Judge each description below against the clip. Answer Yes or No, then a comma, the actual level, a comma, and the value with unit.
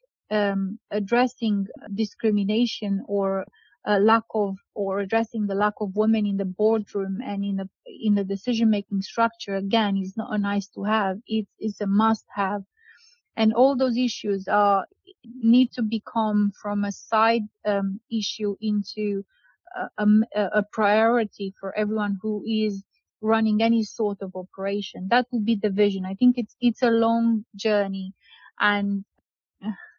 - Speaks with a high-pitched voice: Yes, high, 210 Hz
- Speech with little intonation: Yes, narrow, 2.1 semitones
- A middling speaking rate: Yes, average, 150 wpm